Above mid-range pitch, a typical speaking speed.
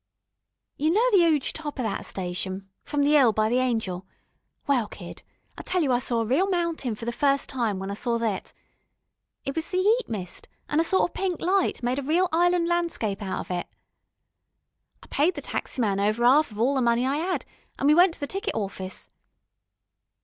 No: very high, 265 Hz; fast, 210 wpm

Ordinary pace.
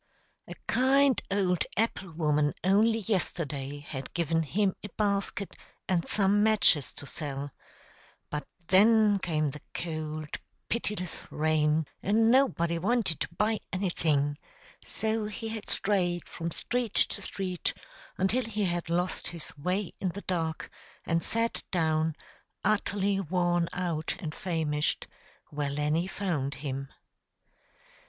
No: slow, 125 wpm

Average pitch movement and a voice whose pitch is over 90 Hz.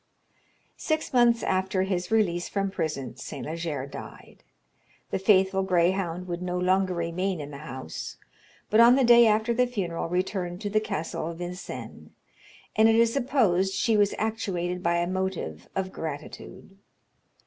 Yes: average, 3.8 semitones; medium, 185 Hz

